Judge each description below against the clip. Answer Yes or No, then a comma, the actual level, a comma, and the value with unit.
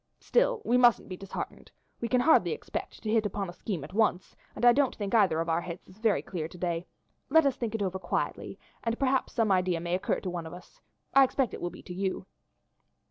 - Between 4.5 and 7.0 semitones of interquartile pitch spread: Yes, average, 5.2 semitones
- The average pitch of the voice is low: No, high, 200 Hz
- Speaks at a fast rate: Yes, fast, 245 wpm